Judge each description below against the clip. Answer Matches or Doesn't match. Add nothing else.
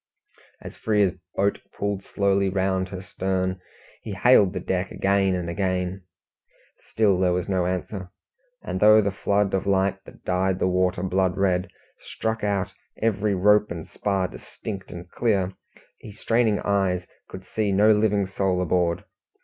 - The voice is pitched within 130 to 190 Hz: Doesn't match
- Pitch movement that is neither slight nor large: Doesn't match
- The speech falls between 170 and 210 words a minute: Doesn't match